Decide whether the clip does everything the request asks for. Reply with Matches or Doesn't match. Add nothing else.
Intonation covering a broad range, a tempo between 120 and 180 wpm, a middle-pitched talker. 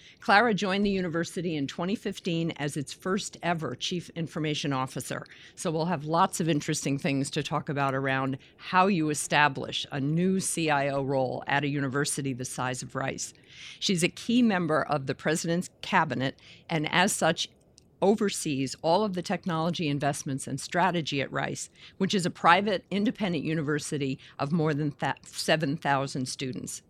Doesn't match